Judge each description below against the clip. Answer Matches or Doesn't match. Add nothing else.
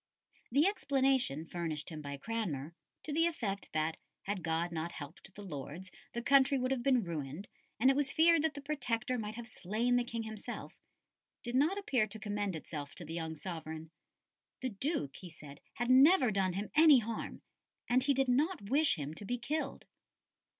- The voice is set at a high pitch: Matches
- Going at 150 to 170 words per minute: Doesn't match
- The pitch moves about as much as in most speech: Doesn't match